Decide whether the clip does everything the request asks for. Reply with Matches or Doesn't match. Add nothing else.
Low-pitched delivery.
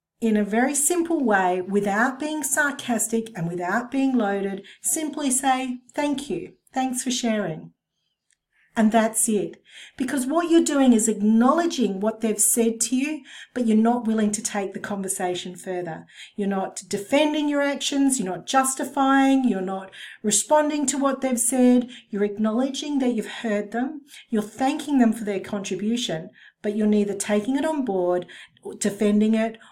Doesn't match